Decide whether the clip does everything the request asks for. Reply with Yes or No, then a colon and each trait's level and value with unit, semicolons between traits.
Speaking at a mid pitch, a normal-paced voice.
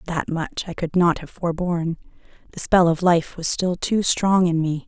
No: medium, 170 Hz; fast, 210 wpm